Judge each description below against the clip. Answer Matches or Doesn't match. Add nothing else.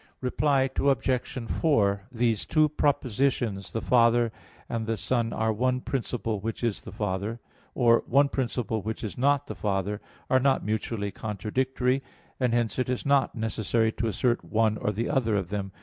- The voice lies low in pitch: Matches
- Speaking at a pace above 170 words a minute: Doesn't match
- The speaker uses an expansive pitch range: Doesn't match